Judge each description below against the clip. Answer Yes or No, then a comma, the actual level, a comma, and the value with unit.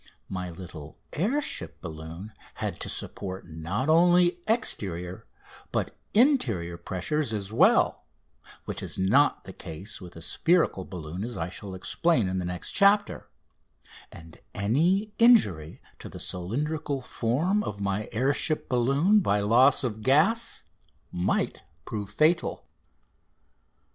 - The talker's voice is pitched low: Yes, low, 110 Hz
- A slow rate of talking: Yes, slow, 130 wpm